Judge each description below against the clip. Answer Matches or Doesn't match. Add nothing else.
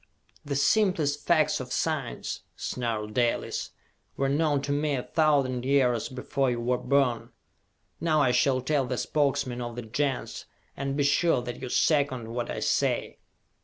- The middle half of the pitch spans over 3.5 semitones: Doesn't match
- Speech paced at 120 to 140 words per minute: Doesn't match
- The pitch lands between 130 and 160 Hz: Matches